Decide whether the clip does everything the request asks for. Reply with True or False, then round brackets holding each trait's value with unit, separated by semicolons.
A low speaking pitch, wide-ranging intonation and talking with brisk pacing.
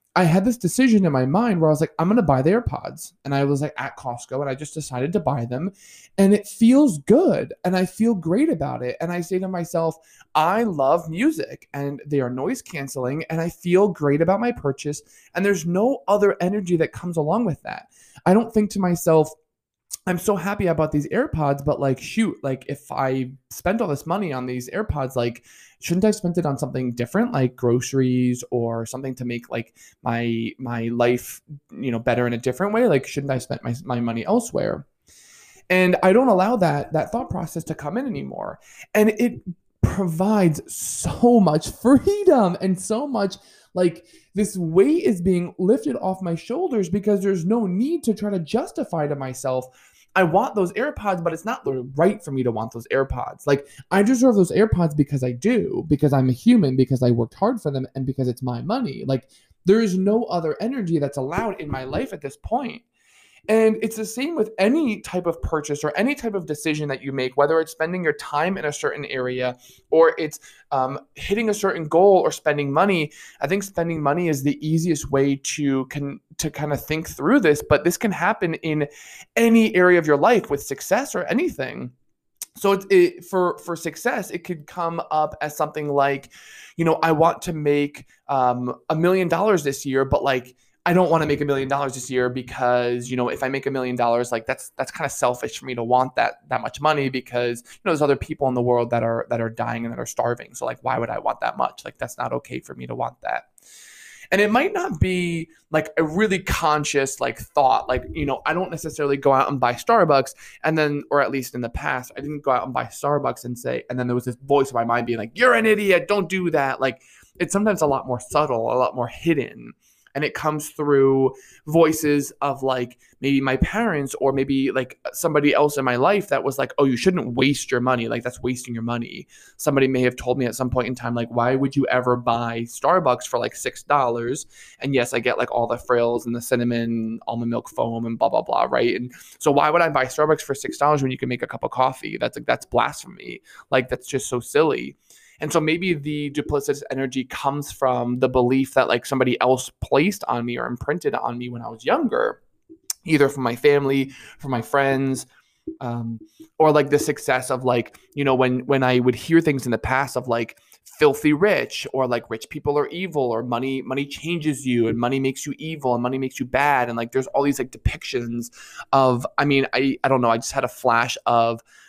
False (145 Hz; 5.9 semitones; 225 wpm)